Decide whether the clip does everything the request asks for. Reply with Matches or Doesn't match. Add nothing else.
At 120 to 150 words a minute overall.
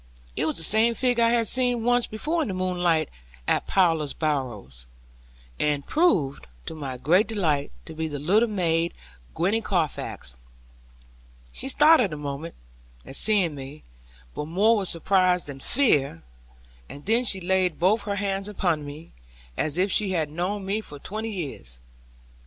Doesn't match